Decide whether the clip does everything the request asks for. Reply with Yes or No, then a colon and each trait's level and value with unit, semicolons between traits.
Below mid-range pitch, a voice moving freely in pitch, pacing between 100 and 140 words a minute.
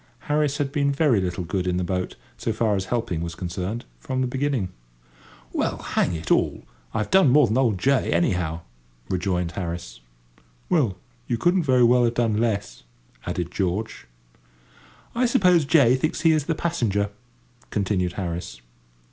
No: low, 110 Hz; wide, 7.4 semitones; average, 160 wpm